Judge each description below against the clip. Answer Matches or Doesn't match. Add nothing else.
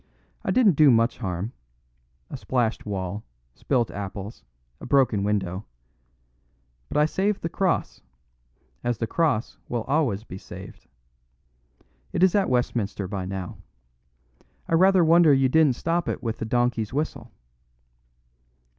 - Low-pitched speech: Matches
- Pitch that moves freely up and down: Matches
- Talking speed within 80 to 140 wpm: Matches